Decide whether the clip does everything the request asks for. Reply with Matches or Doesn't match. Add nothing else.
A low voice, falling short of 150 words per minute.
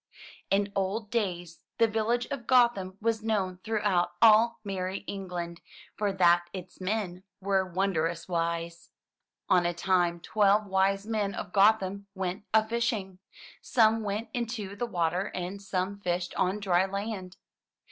Doesn't match